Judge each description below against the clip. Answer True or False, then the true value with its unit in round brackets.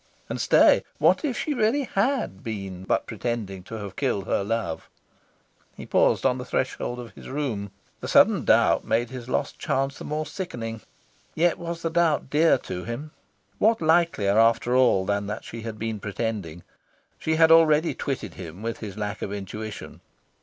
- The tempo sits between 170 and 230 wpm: True (175 wpm)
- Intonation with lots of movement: True (7.2 semitones)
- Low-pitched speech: True (115 Hz)